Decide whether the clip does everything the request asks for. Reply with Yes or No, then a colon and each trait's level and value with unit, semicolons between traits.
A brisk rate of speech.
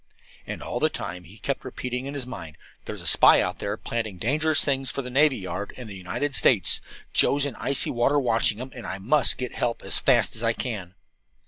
Yes: fast, 225 wpm